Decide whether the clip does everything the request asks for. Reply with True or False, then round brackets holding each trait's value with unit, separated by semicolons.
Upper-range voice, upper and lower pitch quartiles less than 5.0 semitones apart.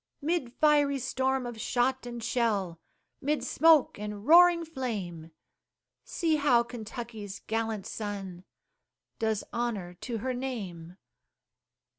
True (235 Hz; 4.5 semitones)